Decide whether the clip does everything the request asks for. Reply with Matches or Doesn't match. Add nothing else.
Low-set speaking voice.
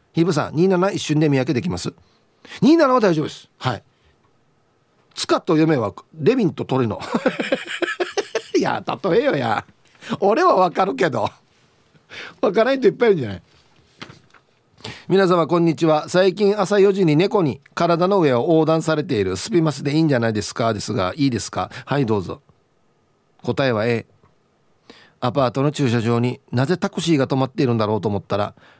Doesn't match